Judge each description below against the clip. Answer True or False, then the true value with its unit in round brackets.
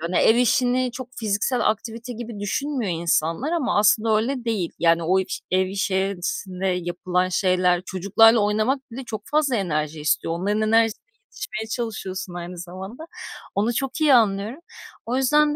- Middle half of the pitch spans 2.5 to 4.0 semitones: False (4.9 semitones)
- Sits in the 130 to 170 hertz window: False (215 Hz)